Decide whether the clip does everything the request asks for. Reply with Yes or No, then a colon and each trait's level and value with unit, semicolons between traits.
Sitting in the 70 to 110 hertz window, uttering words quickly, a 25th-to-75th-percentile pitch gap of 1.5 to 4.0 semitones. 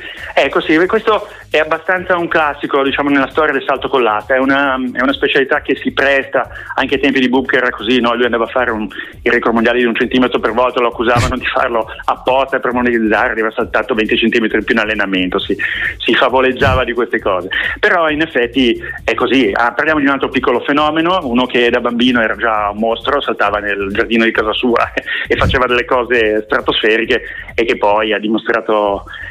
No: low, 125 Hz; fast, 200 wpm; average, 3.3 semitones